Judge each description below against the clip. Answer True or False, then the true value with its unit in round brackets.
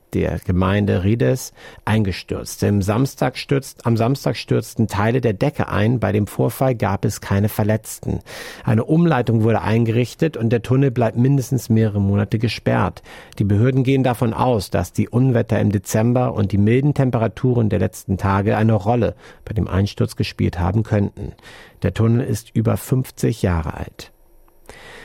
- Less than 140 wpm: False (150 wpm)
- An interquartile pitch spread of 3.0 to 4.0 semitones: True (3.5 semitones)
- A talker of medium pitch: False (110 Hz)